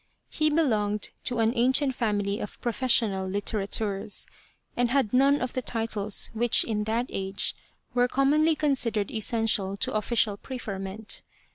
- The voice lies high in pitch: Yes, high, 225 Hz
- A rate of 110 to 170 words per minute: Yes, average, 140 wpm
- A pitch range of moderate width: Yes, average, 3.6 semitones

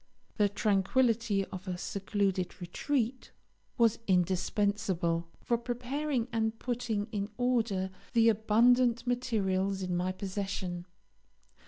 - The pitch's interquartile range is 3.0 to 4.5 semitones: Yes, average, 3.8 semitones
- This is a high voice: Yes, high, 210 Hz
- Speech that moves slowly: Yes, slow, 105 wpm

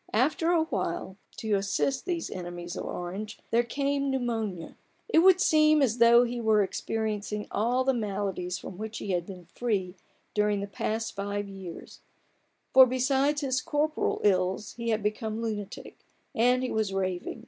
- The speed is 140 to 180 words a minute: Yes, average, 160 wpm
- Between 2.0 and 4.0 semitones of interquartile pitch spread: No, average, 4.7 semitones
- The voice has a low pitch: No, high, 220 Hz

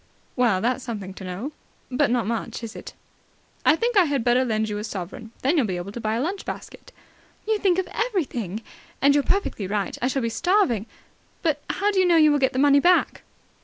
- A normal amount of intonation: No, wide, 7.0 semitones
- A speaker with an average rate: No, fast, 225 wpm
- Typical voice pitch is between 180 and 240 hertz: No, very high, 255 Hz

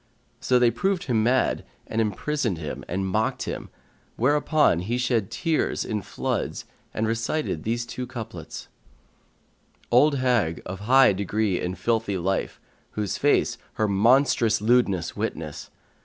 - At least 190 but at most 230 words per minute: No, average, 145 wpm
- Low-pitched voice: Yes, low, 115 Hz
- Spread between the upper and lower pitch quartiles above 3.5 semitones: Yes, average, 4.1 semitones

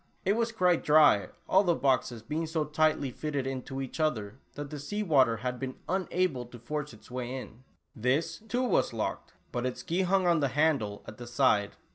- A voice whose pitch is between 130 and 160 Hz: Yes, medium, 140 Hz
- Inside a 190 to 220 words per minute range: Yes, average, 200 wpm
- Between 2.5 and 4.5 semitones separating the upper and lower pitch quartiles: No, average, 5.0 semitones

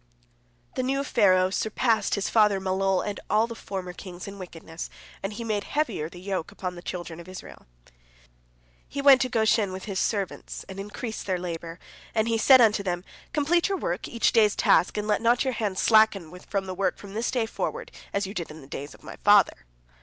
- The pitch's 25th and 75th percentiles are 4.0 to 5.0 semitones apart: No, average, 3.5 semitones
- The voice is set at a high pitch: Yes, high, 200 Hz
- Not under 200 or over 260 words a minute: Yes, fast, 205 wpm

